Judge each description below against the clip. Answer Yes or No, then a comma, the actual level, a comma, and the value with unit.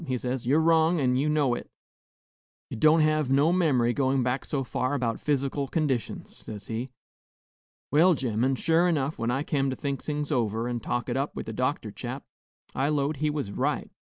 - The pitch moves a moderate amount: Yes, average, 3.5 semitones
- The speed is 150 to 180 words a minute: No, average, 200 wpm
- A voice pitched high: No, low, 135 Hz